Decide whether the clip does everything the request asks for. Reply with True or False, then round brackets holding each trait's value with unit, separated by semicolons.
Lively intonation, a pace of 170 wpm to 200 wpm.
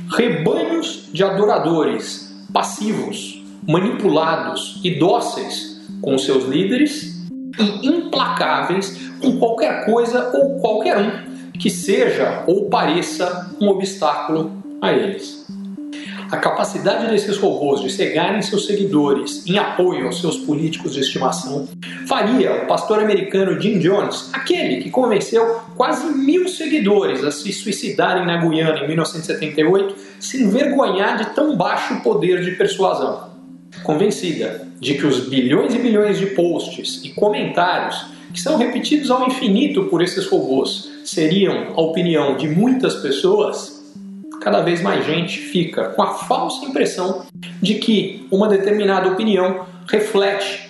False (5.7 semitones; 130 wpm)